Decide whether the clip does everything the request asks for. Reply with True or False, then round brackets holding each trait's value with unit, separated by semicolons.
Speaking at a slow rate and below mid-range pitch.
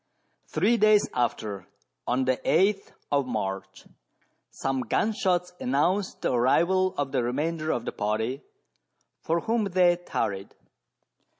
False (125 wpm; 145 Hz)